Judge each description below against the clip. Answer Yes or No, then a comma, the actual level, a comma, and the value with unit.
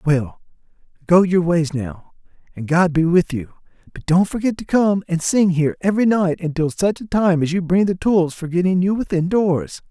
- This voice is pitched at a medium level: Yes, medium, 175 Hz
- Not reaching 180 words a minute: No, average, 200 wpm